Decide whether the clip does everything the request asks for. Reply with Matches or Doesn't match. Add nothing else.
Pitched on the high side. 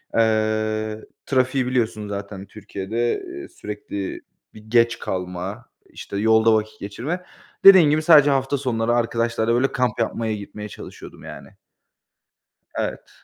Doesn't match